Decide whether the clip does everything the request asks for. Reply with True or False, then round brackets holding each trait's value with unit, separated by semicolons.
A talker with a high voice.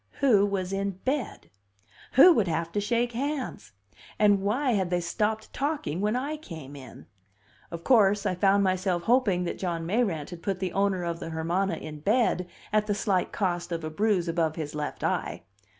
True (195 Hz)